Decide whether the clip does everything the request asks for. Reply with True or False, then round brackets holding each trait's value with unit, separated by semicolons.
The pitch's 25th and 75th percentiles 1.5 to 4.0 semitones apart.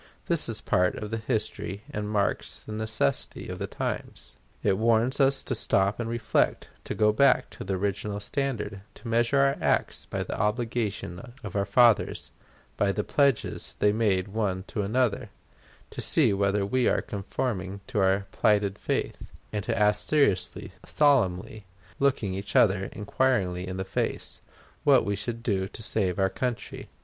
True (3.1 semitones)